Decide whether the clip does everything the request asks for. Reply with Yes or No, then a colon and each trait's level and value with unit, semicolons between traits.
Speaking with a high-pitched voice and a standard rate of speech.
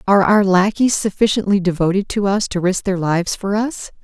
Yes: high, 195 Hz; average, 195 wpm